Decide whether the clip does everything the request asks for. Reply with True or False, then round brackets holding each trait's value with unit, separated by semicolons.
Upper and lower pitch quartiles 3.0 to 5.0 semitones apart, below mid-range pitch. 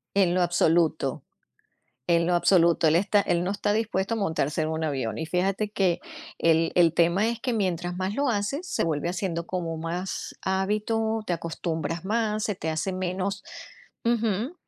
False (3.8 semitones; 185 Hz)